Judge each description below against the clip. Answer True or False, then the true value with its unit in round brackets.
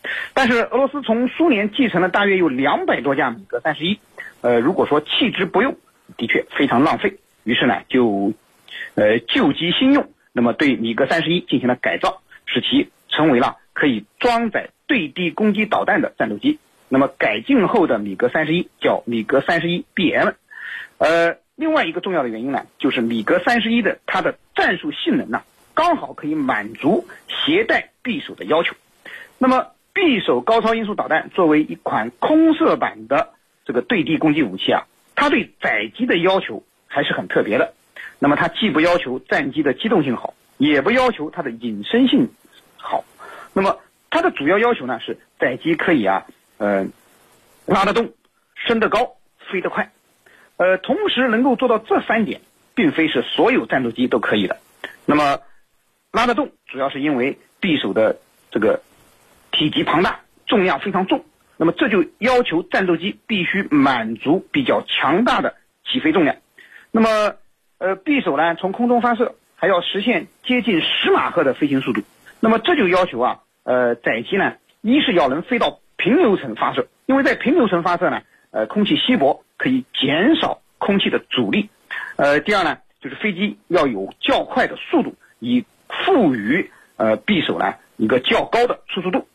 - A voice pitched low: False (230 Hz)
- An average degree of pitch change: False (8.3 semitones)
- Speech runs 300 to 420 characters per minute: False (265 characters per minute)